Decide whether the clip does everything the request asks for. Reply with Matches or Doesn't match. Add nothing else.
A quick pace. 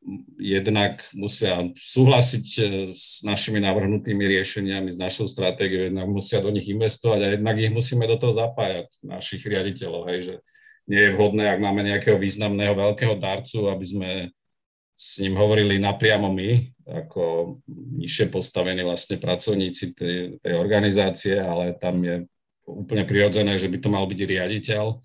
Doesn't match